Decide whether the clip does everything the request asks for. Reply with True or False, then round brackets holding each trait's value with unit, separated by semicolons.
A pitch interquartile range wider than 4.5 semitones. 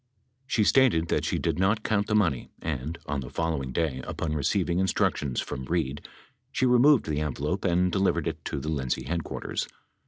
True (5.0 semitones)